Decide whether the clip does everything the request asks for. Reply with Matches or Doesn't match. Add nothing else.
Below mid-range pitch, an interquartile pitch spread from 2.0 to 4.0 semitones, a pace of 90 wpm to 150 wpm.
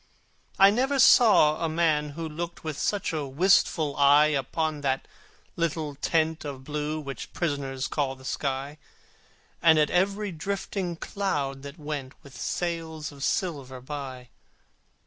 Doesn't match